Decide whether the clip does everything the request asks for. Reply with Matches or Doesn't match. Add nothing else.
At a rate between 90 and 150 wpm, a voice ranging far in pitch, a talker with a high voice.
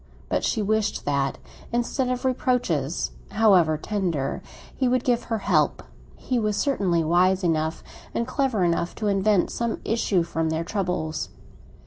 Matches